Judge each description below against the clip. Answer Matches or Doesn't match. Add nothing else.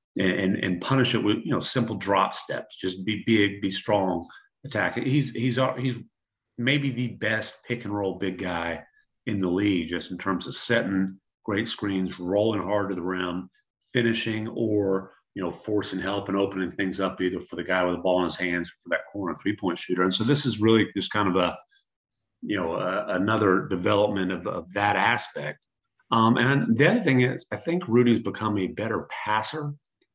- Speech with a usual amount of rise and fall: Matches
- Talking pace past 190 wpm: Matches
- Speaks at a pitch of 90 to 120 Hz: Matches